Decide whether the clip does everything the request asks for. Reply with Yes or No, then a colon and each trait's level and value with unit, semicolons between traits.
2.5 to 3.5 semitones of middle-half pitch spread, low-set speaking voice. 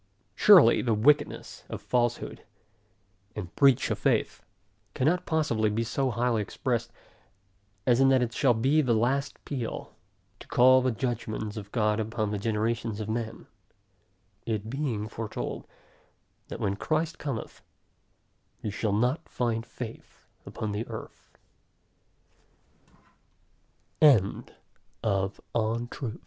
Yes: average, 3.2 semitones; low, 115 Hz